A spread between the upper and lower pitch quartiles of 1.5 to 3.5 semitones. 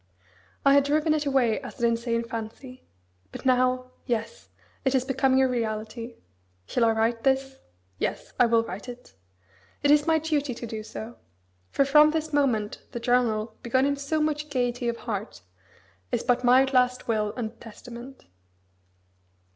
Yes: average, 3.1 semitones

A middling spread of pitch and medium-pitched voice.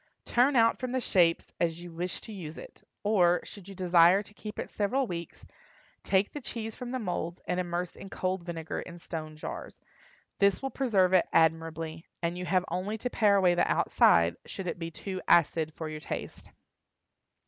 Yes: average, 3.7 semitones; medium, 180 Hz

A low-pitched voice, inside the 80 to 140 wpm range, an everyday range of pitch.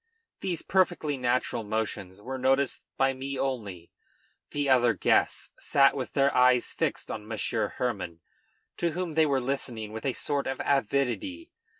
No: low, 130 Hz; average, 155 wpm; average, 3.6 semitones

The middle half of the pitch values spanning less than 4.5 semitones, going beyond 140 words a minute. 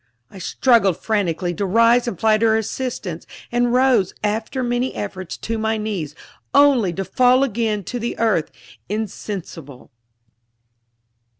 No: average, 4.0 semitones; slow, 135 wpm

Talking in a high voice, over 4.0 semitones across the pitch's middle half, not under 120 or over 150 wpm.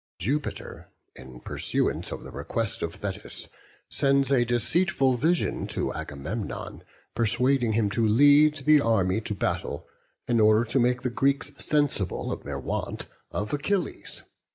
No: low, 120 Hz; average, 4.7 semitones; average, 140 wpm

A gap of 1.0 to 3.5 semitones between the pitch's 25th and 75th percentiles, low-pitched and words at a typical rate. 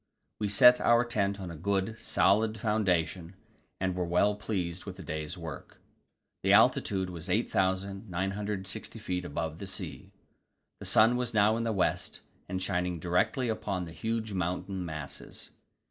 Yes: average, 3.2 semitones; very low, 95 Hz; average, 150 wpm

